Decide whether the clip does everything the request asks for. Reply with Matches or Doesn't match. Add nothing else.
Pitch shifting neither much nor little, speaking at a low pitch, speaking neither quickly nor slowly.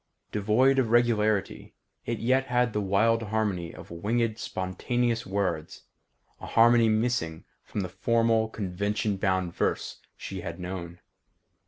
Doesn't match